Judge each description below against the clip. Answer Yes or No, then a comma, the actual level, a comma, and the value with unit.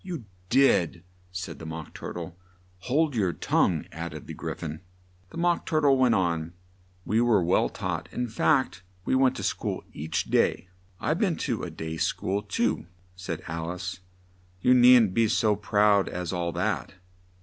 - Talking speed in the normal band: Yes, average, 175 wpm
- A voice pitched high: No, very low, 95 Hz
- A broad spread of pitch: Yes, wide, 6.4 semitones